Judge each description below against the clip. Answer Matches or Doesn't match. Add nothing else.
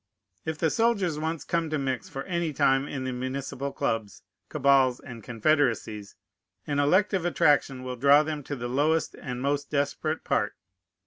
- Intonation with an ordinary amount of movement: Matches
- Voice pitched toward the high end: Doesn't match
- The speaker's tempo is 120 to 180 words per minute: Matches